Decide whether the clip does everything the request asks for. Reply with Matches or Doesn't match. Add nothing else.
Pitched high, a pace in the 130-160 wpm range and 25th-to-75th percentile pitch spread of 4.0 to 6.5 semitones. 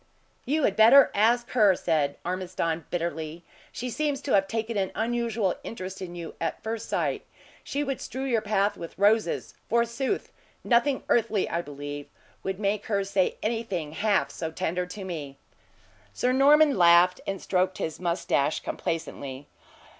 Matches